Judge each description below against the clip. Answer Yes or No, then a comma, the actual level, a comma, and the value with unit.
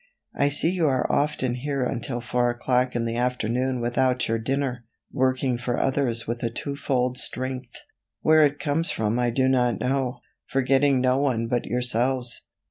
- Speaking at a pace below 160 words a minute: No, average, 170 wpm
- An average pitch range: No, narrow, 2.0 semitones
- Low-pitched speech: Yes, low, 125 Hz